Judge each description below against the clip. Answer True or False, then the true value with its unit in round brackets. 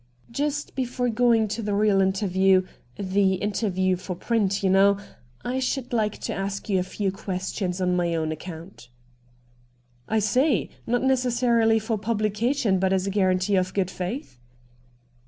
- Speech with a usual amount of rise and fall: True (3.5 semitones)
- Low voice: False (195 Hz)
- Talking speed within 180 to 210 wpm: False (170 wpm)